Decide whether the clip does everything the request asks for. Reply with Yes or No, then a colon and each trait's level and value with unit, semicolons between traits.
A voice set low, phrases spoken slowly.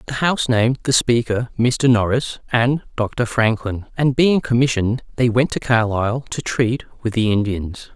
No: low, 120 Hz; average, 165 wpm